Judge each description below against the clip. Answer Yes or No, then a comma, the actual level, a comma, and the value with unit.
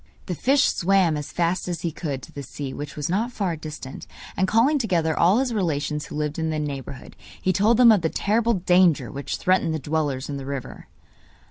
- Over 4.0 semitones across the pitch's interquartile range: Yes, average, 4.9 semitones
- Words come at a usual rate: No, fast, 215 wpm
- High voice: No, medium, 165 Hz